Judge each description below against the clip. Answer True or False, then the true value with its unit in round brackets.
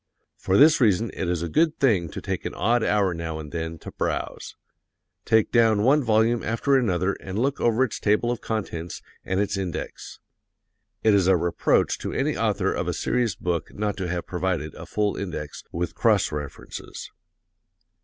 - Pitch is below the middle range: True (100 Hz)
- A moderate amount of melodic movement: True (4.7 semitones)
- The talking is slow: False (185 wpm)